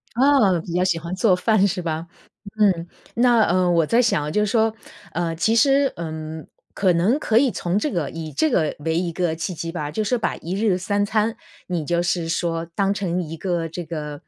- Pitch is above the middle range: No, medium, 180 Hz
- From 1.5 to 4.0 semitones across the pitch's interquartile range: No, average, 4.4 semitones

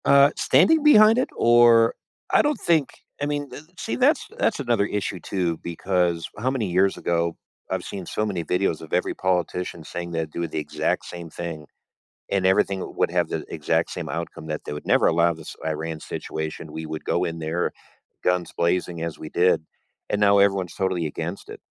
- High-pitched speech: No, very low, 90 Hz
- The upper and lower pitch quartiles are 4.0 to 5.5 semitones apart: Yes, average, 4.5 semitones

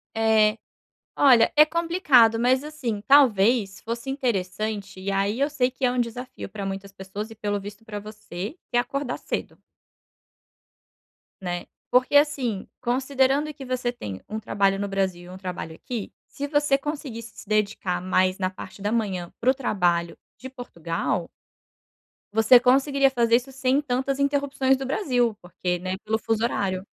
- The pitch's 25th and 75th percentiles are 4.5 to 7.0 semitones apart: Yes, average, 5.2 semitones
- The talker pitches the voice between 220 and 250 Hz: Yes, high, 230 Hz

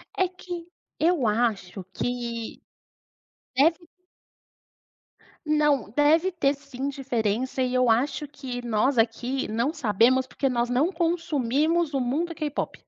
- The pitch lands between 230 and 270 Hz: Yes, very high, 265 Hz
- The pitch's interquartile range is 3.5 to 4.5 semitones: Yes, average, 4.2 semitones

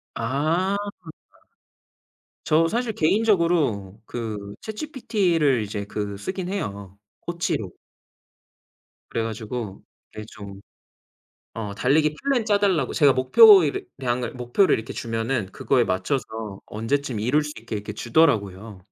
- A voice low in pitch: Yes, low, 130 Hz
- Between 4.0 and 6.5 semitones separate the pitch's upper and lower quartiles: No, wide, 8.1 semitones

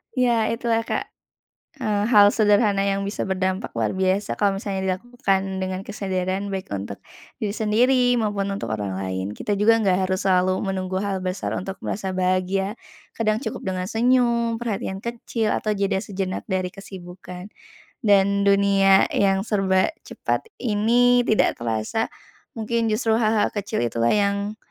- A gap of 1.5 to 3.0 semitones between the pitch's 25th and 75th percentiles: Yes, narrow, 2.6 semitones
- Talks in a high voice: Yes, high, 200 Hz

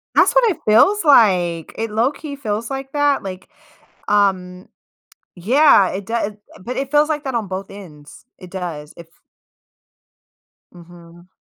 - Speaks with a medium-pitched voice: No, high, 205 Hz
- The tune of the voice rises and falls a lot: Yes, wide, 7.0 semitones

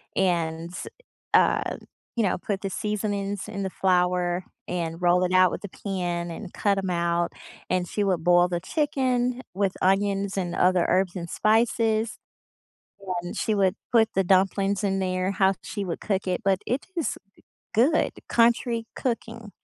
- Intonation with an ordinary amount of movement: Yes, average, 3.0 semitones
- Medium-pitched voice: No, high, 195 Hz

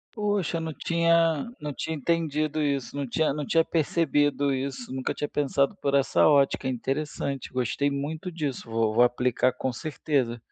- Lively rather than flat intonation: No, average, 3.3 semitones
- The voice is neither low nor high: Yes, medium, 145 Hz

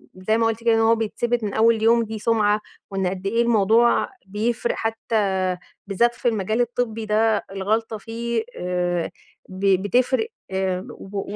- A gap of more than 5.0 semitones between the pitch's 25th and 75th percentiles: No, average, 2.8 semitones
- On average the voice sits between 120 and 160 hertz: No, high, 220 Hz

